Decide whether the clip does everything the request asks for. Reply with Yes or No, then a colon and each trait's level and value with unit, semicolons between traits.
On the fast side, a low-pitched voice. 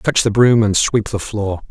Yes: fast, 245 wpm; low, 105 Hz